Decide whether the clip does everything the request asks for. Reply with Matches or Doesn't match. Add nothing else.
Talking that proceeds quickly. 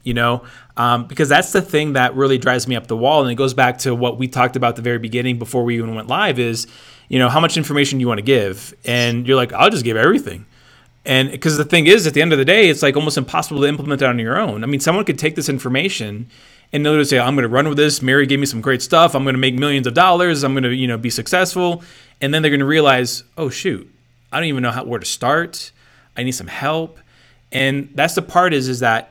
Matches